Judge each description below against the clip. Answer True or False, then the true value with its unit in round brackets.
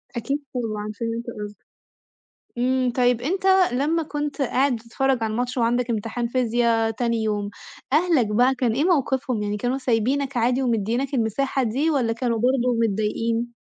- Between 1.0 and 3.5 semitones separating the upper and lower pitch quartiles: True (2.8 semitones)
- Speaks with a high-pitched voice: True (245 Hz)